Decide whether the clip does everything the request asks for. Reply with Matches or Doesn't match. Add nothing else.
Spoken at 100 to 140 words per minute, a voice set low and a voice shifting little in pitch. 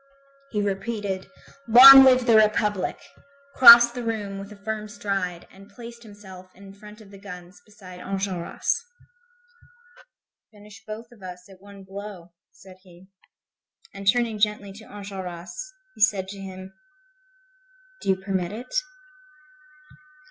Doesn't match